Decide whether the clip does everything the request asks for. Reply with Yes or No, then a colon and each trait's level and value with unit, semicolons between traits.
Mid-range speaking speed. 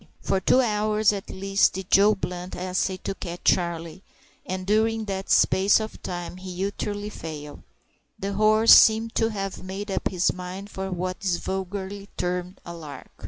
Yes: average, 165 wpm